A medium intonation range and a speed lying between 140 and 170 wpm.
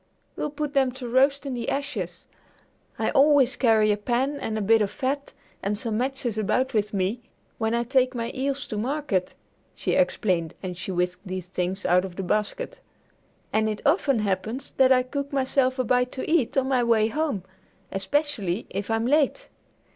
No: average, 4.8 semitones; average, 185 wpm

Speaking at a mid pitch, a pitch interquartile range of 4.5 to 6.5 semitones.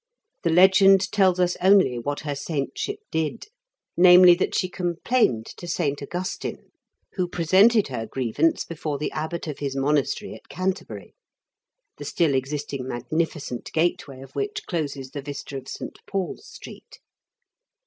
Yes: medium, 160 Hz; average, 4.8 semitones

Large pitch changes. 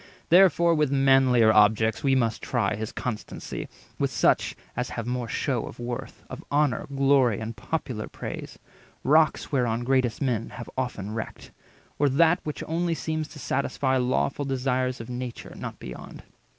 No: average, 3.5 semitones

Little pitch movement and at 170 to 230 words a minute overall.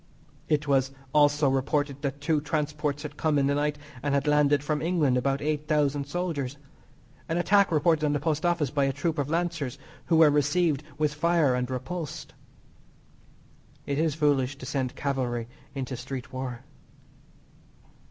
No: narrow, 2.1 semitones; average, 160 wpm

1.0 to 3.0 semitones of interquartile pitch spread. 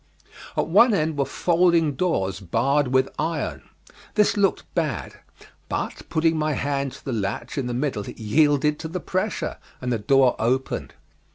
No: average, 4.4 semitones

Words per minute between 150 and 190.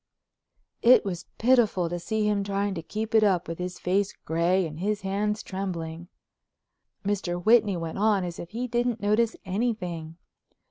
Yes: average, 165 wpm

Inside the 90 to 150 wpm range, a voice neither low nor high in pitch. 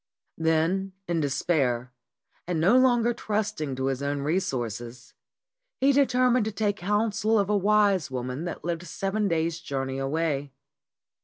Yes: average, 140 wpm; medium, 170 Hz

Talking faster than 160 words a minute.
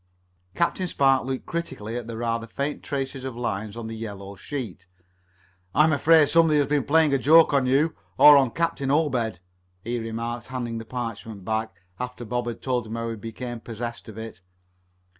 Yes: average, 180 wpm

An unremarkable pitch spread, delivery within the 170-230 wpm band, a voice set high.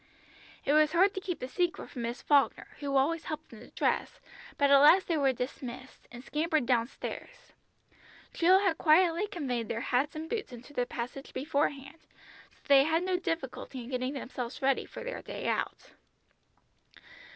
Yes: average, 4.6 semitones; average, 180 wpm; very high, 285 Hz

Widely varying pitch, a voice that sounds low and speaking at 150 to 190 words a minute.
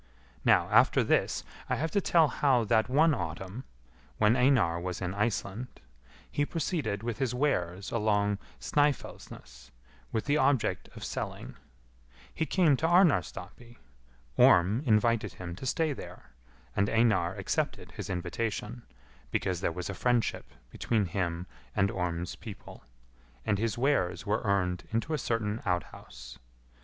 No: wide, 5.8 semitones; low, 110 Hz; slow, 135 wpm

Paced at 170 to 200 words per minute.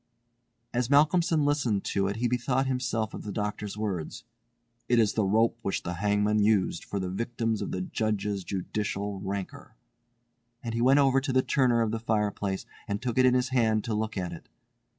Yes: average, 190 wpm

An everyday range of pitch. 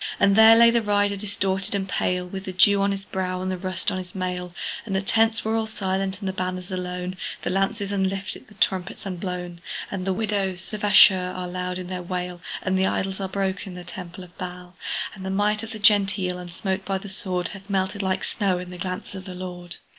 No: narrow, 1.6 semitones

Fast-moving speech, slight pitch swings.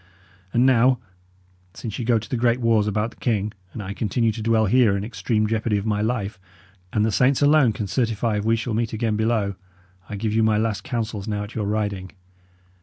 Yes: fast, 215 wpm; narrow, 1.9 semitones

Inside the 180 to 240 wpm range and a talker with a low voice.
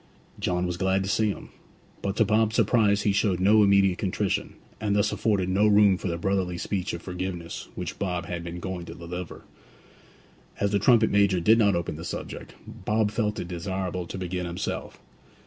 Yes: average, 190 wpm; very low, 95 Hz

